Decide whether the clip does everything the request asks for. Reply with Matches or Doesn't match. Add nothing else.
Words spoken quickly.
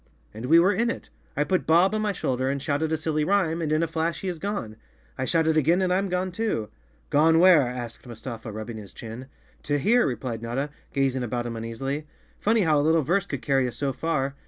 Matches